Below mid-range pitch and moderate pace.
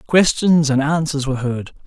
No: medium, 145 Hz; average, 160 wpm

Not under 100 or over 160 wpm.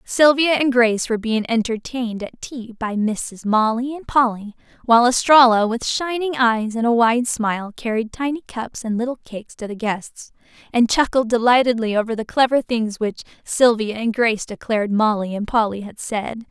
No: average, 175 wpm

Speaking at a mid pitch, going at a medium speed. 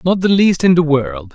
No: medium, 175 Hz; fast, 270 wpm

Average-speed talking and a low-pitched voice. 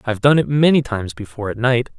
No: fast, 240 wpm; low, 120 Hz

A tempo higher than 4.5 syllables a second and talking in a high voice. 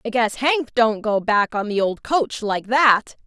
No: 4.0 syllables/s; high, 230 Hz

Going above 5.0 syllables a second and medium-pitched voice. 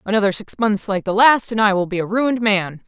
No: 5.8 syllables/s; high, 210 Hz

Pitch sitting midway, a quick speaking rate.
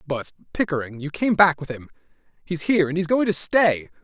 Yes: medium, 165 Hz; fast, 210 wpm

